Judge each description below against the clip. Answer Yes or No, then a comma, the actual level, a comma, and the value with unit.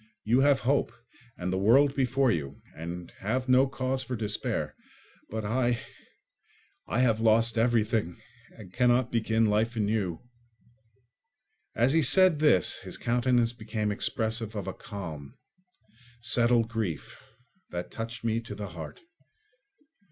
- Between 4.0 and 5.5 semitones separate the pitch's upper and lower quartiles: No, average, 3.2 semitones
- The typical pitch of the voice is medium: No, low, 115 Hz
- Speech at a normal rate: No, slow, 130 wpm